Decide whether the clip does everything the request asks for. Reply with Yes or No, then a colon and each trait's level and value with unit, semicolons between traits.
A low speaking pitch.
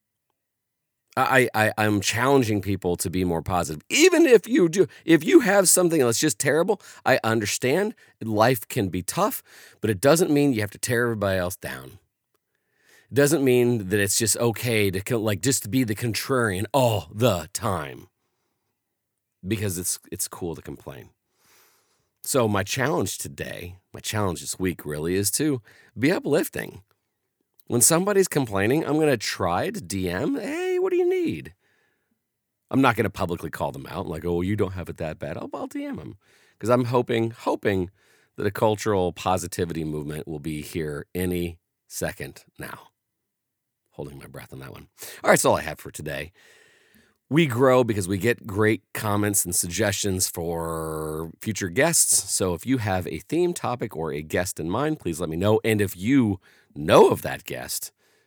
Yes: low, 110 Hz